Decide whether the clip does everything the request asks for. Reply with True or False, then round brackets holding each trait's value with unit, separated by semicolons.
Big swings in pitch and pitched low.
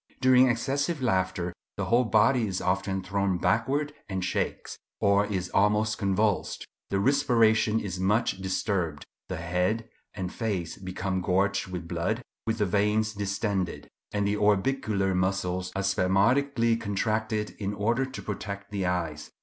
False (3.1 semitones; 100 Hz)